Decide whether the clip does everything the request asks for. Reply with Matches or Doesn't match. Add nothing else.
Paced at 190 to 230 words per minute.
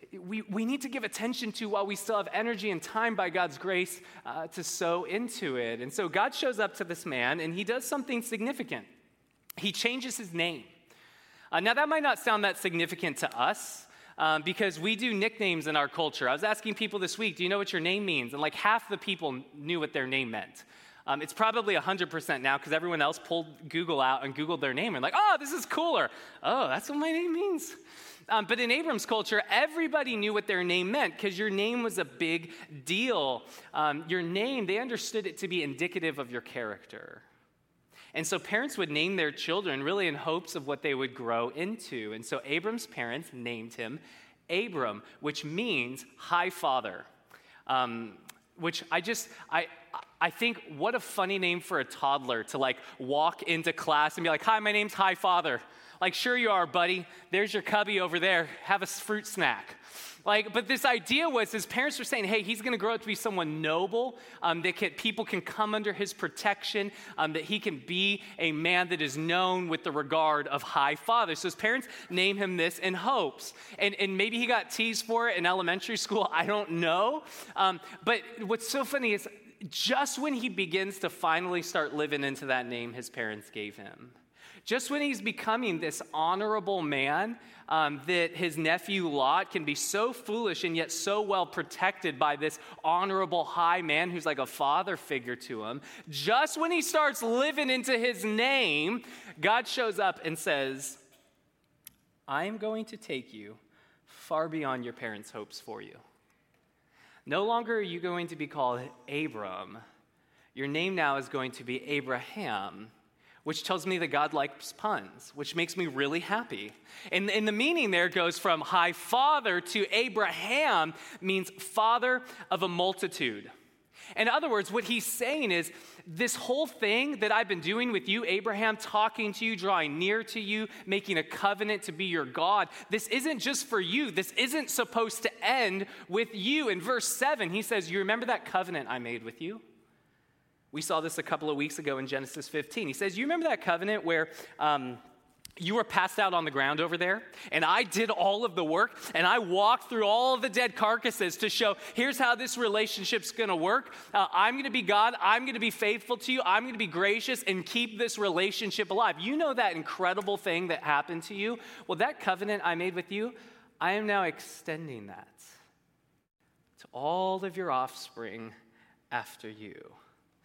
Matches